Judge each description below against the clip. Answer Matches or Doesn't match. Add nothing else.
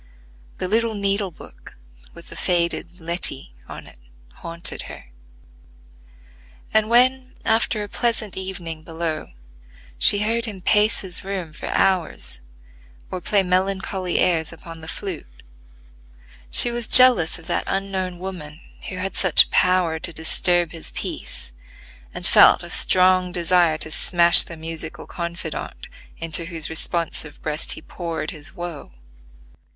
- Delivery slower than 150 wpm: Matches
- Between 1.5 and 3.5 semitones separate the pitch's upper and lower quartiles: Matches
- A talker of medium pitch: Matches